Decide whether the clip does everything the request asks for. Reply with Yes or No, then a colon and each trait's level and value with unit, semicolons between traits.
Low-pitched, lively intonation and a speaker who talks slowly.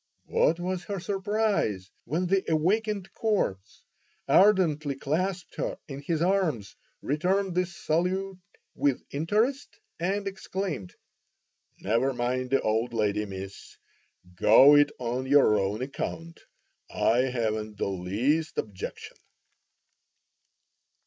No: medium, 150 Hz; wide, 8.4 semitones; slow, 110 wpm